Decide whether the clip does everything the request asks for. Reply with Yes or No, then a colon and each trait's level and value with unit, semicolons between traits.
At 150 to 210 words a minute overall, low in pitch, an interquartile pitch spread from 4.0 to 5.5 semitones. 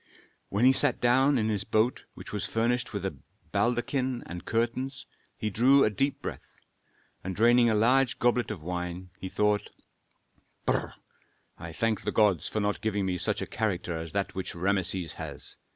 Yes: average, 170 wpm; low, 110 Hz; average, 4.5 semitones